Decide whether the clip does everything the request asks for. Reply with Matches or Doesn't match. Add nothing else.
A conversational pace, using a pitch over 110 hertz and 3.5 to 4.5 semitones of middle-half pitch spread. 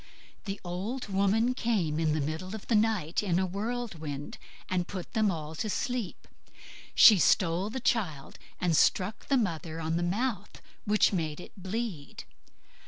Doesn't match